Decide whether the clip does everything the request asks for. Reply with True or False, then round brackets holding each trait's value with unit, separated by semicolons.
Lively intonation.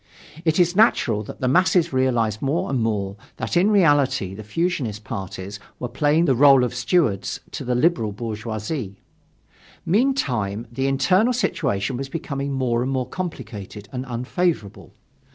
True (7.1 semitones)